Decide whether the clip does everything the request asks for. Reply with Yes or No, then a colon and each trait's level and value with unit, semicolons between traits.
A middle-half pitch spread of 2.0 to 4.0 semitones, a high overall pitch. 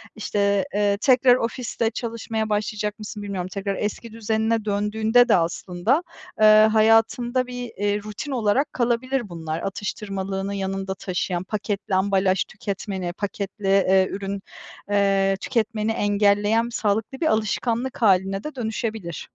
Yes: narrow, 2.5 semitones; high, 210 Hz